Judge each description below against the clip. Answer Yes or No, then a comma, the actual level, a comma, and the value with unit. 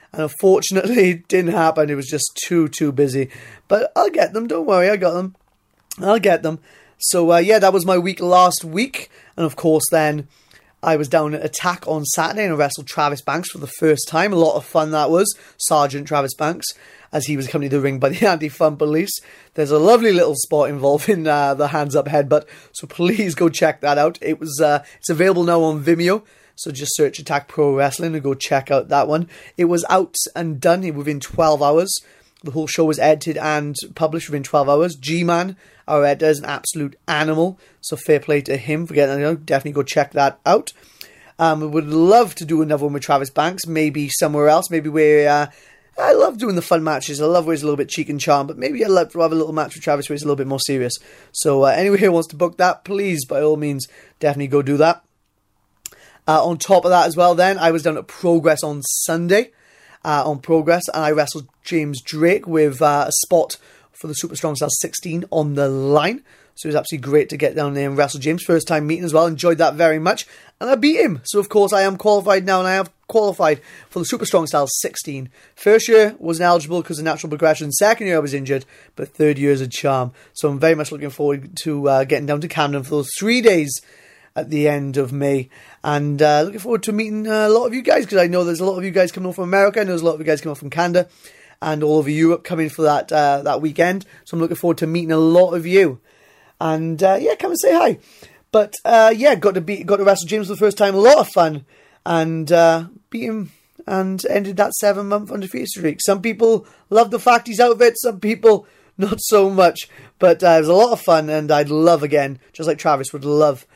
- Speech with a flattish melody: No, average, 3.7 semitones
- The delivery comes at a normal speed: No, fast, 245 wpm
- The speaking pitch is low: No, medium, 160 Hz